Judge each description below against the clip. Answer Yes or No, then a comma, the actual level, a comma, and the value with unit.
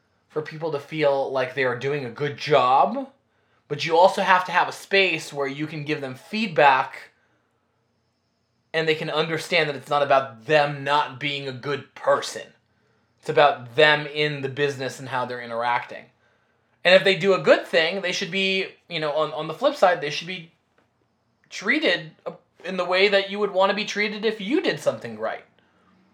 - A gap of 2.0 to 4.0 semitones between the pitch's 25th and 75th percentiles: No, wide, 5.5 semitones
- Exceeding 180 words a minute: Yes, average, 195 wpm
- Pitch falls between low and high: Yes, medium, 150 Hz